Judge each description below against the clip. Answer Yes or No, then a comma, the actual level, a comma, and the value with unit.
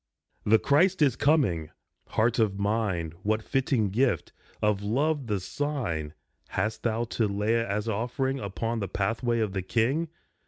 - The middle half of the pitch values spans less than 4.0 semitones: No, average, 4.3 semitones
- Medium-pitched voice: No, low, 110 Hz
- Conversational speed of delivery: Yes, average, 150 wpm